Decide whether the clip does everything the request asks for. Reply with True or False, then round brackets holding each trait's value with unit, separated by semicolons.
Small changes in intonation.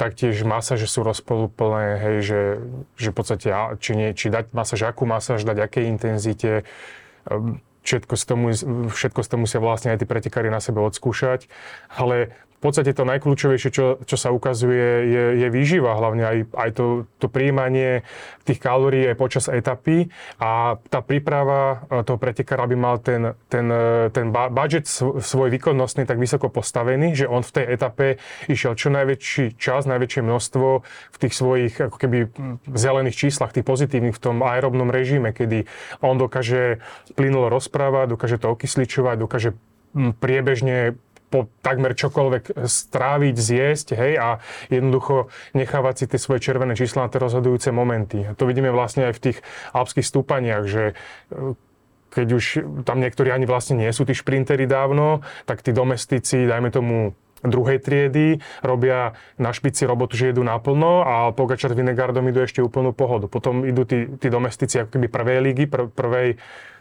True (2.1 semitones)